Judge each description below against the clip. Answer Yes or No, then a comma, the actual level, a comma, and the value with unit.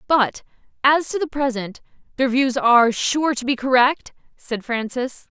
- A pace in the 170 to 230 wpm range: No, average, 155 wpm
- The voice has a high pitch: Yes, very high, 255 Hz